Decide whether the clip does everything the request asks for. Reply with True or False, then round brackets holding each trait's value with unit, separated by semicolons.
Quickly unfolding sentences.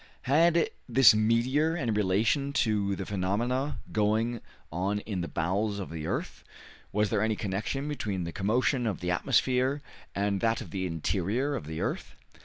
False (165 wpm)